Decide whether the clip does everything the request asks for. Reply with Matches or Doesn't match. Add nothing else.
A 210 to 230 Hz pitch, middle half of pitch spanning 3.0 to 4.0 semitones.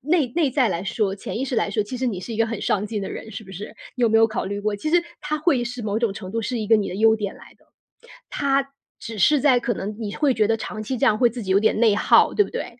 Matches